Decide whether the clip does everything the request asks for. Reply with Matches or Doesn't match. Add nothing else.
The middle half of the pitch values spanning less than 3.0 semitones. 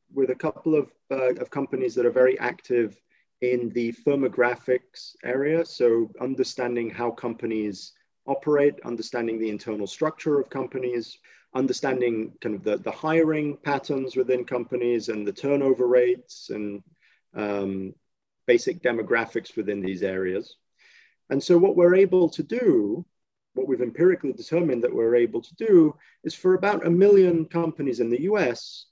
Doesn't match